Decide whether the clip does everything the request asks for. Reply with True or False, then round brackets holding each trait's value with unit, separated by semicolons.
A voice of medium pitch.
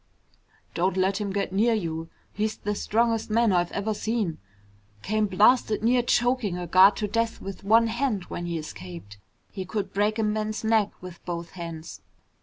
False (205 Hz)